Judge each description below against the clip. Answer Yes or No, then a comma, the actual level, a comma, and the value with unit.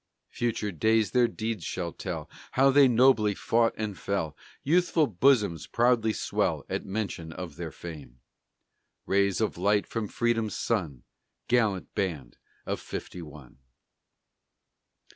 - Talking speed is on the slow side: Yes, slow, 125 wpm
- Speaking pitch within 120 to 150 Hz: No, low, 105 Hz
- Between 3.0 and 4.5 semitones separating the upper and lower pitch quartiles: No, average, 5.1 semitones